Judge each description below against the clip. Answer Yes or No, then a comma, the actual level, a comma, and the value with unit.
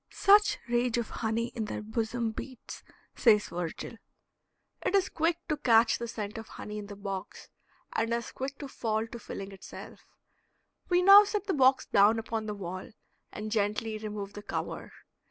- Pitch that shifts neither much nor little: Yes, average, 3.5 semitones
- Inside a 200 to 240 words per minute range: No, average, 175 wpm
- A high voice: Yes, high, 225 Hz